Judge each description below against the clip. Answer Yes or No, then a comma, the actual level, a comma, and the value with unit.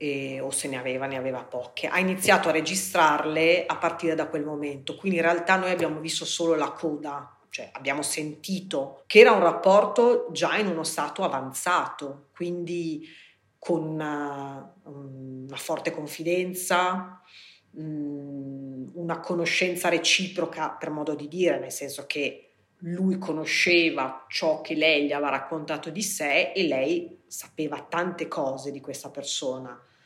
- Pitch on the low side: No, medium, 160 Hz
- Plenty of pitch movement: No, average, 3.6 semitones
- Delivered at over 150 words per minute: No, average, 145 wpm